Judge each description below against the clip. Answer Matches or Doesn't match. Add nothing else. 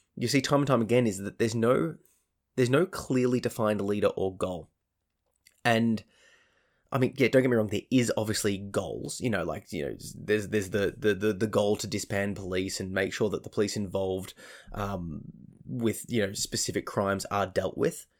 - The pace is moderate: Matches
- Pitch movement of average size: Matches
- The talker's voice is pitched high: Doesn't match